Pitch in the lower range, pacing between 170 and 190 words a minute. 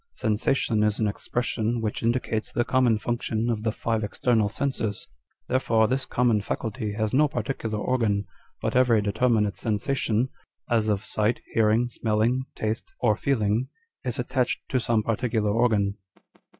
No: low, 115 Hz; average, 150 wpm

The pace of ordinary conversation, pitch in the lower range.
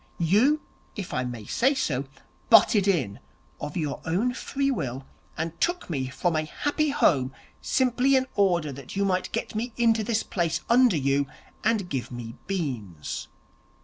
No: average, 160 wpm; medium, 180 Hz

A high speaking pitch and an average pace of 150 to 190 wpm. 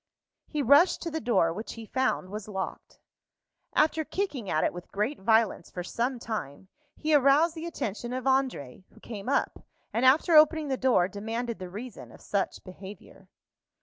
Yes: high, 235 Hz; average, 175 wpm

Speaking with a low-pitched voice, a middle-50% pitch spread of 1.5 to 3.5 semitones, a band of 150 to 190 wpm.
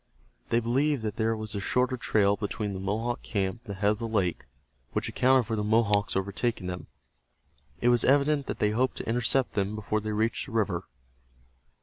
No: low, 110 Hz; average, 2.9 semitones; average, 200 wpm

